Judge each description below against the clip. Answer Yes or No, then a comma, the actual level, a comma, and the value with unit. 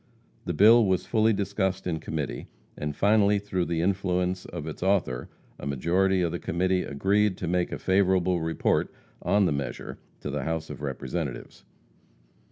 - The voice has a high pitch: No, very low, 90 Hz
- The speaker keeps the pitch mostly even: No, average, 3.2 semitones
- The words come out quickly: No, average, 165 wpm